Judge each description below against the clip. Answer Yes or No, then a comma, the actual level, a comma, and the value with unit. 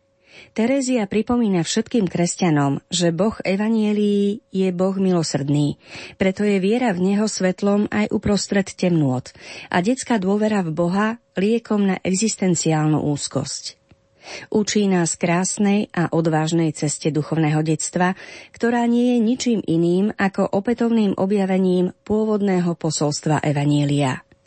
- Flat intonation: No, average, 4.6 semitones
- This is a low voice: No, high, 190 Hz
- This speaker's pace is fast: No, average, 115 wpm